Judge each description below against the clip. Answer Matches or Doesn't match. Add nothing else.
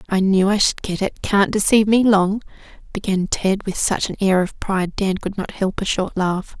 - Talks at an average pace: Doesn't match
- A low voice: Doesn't match